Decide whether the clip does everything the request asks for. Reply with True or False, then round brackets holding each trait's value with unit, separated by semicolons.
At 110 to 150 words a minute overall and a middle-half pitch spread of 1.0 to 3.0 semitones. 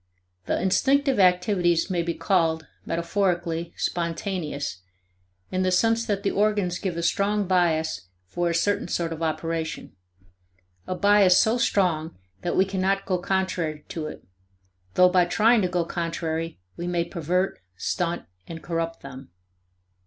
True (145 wpm; 2.7 semitones)